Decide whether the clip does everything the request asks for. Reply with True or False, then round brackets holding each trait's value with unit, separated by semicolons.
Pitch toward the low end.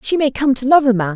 False (255 Hz)